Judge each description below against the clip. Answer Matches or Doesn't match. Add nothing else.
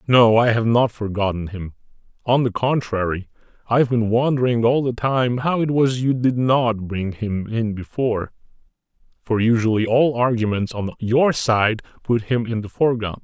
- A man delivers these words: Matches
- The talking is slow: Doesn't match